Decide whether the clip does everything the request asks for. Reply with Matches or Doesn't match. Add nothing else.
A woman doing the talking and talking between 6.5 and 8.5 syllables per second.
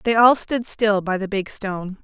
Doesn't match